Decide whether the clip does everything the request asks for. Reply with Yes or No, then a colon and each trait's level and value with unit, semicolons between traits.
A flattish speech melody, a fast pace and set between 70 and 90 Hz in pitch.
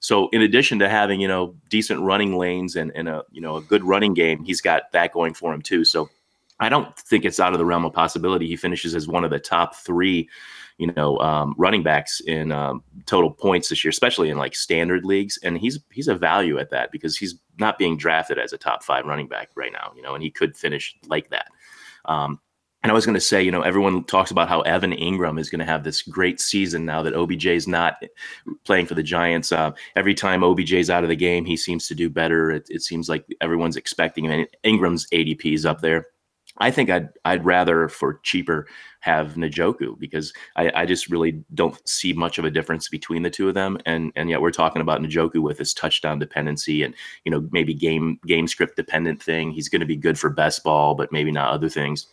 Yes: narrow, 2.2 semitones; fast, 235 wpm; very low, 85 Hz